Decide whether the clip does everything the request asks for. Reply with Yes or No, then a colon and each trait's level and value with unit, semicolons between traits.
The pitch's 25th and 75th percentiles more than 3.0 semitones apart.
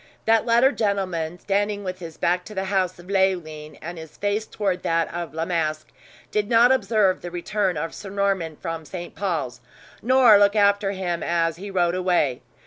Yes: average, 3.4 semitones